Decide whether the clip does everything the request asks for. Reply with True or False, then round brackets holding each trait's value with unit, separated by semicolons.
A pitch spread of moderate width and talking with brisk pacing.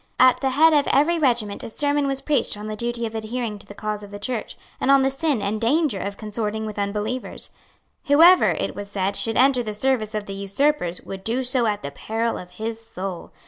True (4.5 semitones; 225 wpm)